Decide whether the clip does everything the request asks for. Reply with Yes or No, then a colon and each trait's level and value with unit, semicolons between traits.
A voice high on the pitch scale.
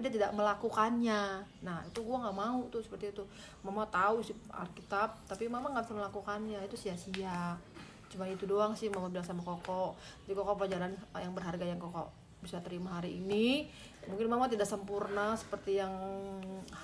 Yes: high, 200 Hz